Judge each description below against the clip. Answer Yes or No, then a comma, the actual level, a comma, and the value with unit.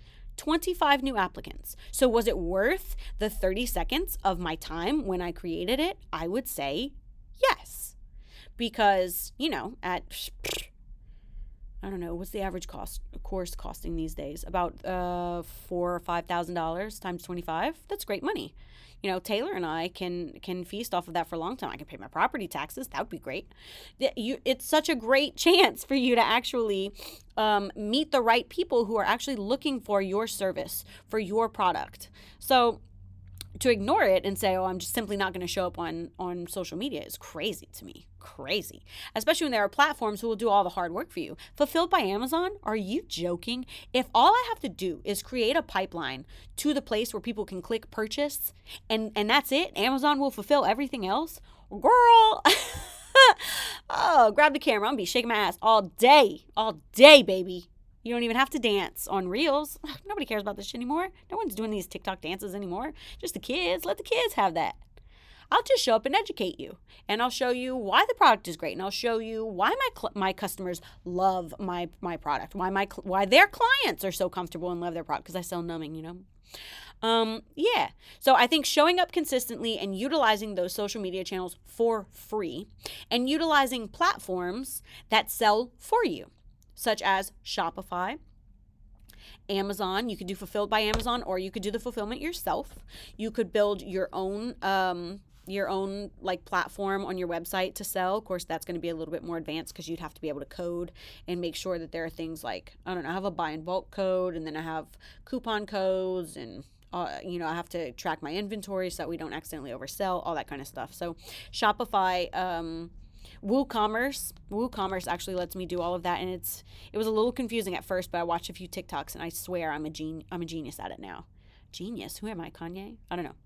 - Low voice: No, high, 195 Hz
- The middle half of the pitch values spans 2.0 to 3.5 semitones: No, wide, 5.4 semitones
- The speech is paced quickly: Yes, fast, 210 wpm